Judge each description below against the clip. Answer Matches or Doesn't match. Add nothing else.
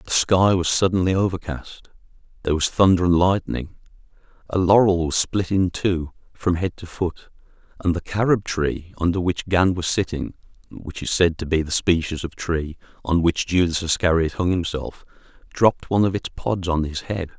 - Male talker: Matches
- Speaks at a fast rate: Doesn't match